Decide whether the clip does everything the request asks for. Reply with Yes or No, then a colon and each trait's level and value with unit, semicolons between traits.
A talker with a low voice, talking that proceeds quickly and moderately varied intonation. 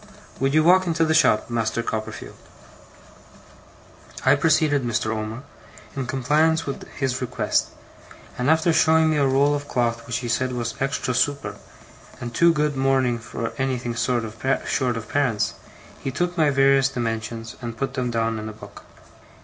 No: low, 130 Hz; average, 160 wpm; average, 3.6 semitones